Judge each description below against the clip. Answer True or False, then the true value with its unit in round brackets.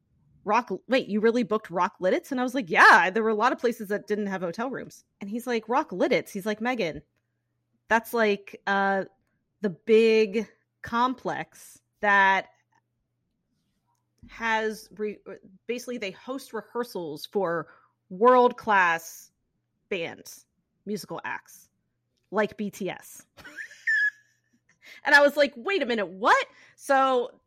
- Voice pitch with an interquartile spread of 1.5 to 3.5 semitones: False (4.0 semitones)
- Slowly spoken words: True (130 wpm)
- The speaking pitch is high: True (215 Hz)